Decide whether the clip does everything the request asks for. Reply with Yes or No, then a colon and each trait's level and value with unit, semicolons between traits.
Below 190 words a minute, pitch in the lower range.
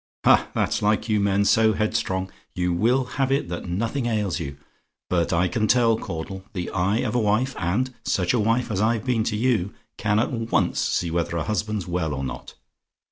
No: average, 200 wpm; low, 105 Hz